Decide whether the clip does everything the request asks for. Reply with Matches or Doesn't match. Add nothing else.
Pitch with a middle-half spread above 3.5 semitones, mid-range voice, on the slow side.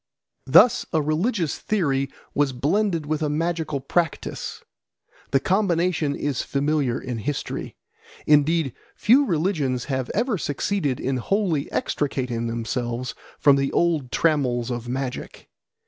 Matches